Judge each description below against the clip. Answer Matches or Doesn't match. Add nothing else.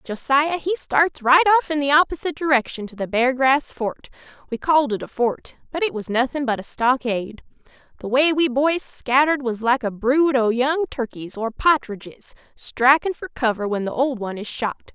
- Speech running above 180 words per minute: Matches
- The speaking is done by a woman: Matches